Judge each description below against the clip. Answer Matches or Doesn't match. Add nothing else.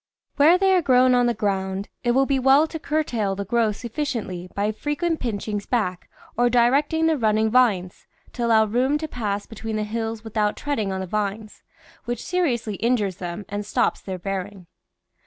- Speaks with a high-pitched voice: Matches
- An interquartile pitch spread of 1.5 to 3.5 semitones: Doesn't match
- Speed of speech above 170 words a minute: Matches